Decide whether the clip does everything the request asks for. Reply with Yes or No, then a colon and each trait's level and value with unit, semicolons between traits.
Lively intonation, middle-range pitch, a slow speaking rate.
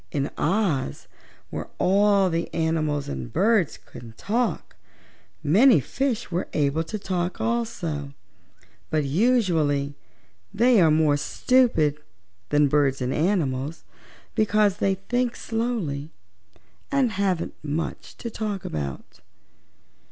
Yes: wide, 6.7 semitones; medium, 170 Hz; slow, 110 wpm